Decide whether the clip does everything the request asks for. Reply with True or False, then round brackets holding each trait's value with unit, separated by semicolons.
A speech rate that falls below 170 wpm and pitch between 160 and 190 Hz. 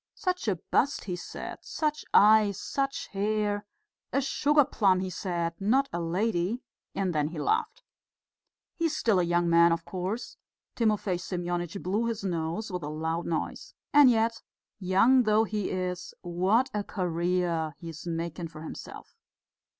True (160 wpm; 185 Hz)